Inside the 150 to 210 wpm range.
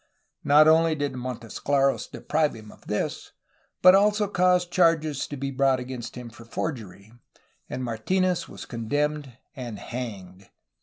No: average, 140 wpm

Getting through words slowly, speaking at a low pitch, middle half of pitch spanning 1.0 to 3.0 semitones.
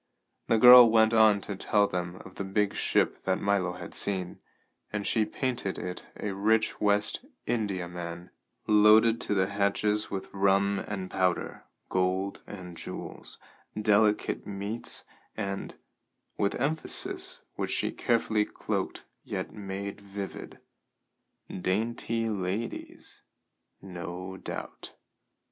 Yes: slow, 120 wpm; low, 100 Hz; narrow, 2.4 semitones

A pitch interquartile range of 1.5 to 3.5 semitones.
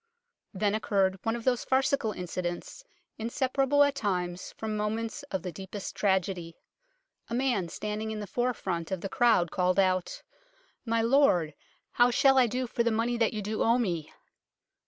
No: average, 4.5 semitones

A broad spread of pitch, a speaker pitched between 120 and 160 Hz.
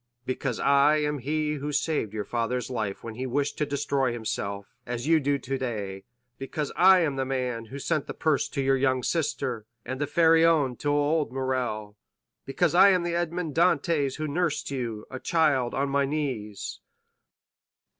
No: average, 3.8 semitones; low, 135 Hz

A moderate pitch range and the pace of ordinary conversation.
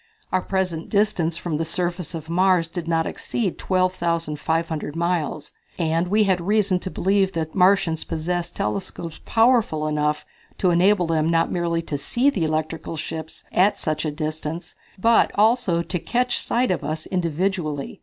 Yes: average, 3.0 semitones; average, 155 wpm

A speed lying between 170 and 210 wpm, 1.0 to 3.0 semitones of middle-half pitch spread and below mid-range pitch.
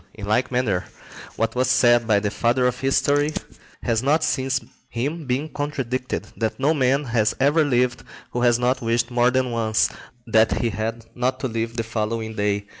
Yes: average, 185 wpm; narrow, 2.5 semitones; low, 120 Hz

